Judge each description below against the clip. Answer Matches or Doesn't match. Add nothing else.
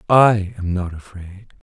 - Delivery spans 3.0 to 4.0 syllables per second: Matches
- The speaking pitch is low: Matches